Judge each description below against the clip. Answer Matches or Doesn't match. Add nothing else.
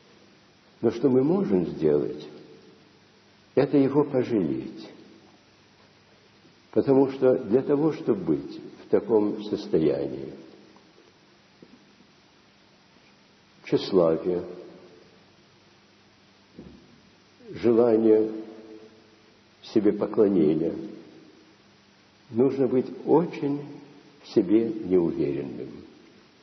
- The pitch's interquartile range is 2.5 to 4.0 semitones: Doesn't match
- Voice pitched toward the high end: Doesn't match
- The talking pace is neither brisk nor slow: Doesn't match